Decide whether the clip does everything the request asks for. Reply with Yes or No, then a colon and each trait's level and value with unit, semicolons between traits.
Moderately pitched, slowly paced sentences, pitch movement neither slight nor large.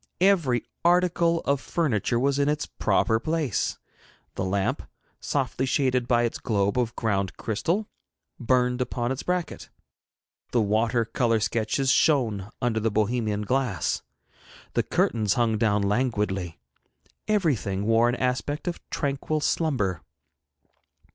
No: low, 120 Hz; slow, 125 wpm; average, 4.7 semitones